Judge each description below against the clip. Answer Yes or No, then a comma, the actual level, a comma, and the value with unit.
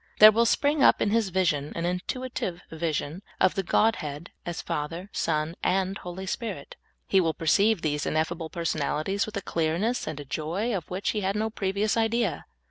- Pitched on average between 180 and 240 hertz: Yes, medium, 185 Hz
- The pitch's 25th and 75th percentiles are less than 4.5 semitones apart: No, average, 4.8 semitones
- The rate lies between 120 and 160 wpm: No, average, 175 wpm